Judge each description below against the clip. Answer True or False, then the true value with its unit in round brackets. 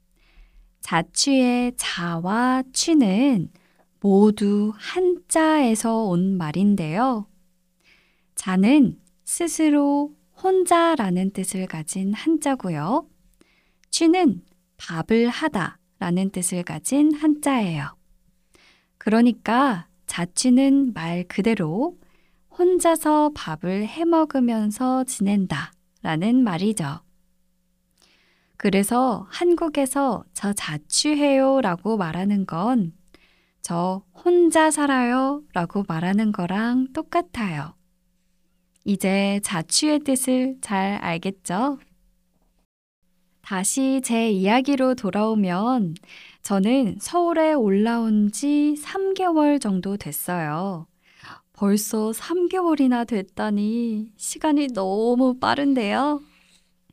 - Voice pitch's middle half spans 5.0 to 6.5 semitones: False (7.0 semitones)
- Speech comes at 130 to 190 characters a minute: True (180 characters per minute)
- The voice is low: False (210 Hz)